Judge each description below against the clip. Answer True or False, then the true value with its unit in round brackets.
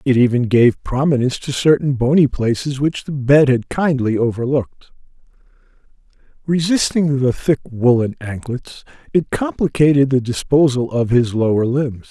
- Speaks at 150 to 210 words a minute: False (135 wpm)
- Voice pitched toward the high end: False (135 Hz)